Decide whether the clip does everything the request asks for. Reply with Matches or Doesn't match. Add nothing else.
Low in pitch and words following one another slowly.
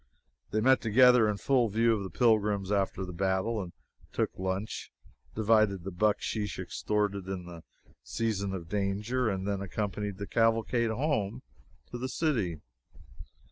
Doesn't match